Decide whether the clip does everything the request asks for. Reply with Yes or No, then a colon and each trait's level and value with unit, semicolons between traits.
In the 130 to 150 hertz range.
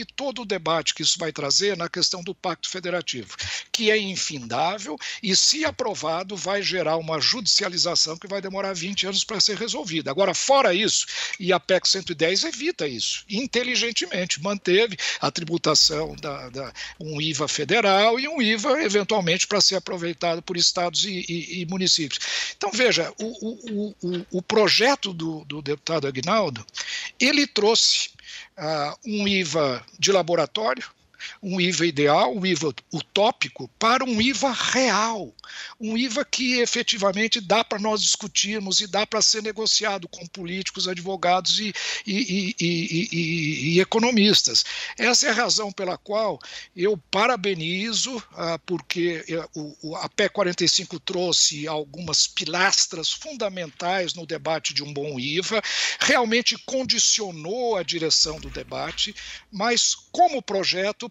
No: high, 190 Hz